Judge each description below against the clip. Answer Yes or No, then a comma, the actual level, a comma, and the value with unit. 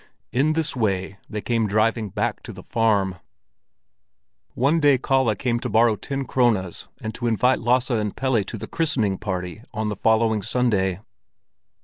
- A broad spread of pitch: No, average, 3.5 semitones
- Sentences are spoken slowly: No, average, 160 wpm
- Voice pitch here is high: No, low, 115 Hz